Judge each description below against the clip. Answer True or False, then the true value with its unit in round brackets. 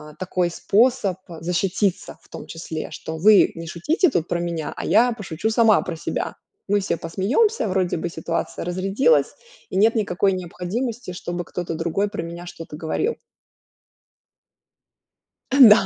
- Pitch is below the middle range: False (185 Hz)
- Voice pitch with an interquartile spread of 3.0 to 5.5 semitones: True (4.2 semitones)